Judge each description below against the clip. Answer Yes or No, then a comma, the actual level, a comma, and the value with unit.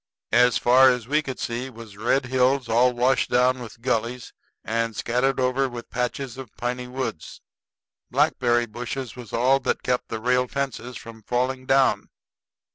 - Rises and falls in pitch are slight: Yes, narrow, 1.7 semitones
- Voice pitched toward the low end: Yes, low, 125 Hz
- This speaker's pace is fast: No, average, 160 wpm